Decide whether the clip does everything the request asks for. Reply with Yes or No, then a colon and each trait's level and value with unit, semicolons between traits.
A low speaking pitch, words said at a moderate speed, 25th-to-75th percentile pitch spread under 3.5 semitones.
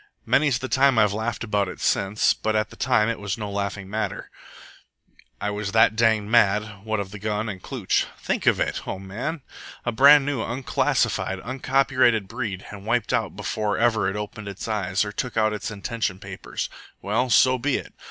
Yes: low, 110 Hz; average, 190 wpm; average, 2.8 semitones